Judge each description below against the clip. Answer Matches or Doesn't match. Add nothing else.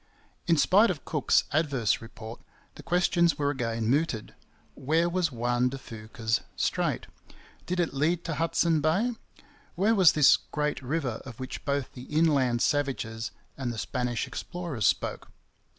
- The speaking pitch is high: Doesn't match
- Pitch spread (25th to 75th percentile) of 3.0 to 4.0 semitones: Doesn't match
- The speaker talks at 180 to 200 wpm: Doesn't match